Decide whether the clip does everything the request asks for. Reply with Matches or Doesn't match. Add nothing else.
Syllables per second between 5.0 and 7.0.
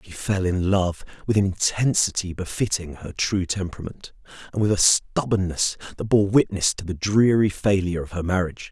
Matches